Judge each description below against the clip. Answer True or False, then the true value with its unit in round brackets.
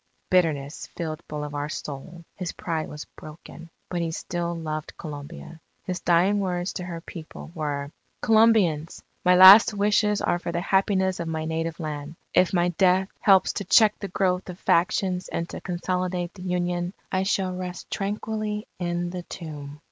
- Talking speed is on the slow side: False (165 wpm)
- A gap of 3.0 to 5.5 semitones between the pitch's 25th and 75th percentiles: False (2.6 semitones)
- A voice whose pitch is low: False (175 Hz)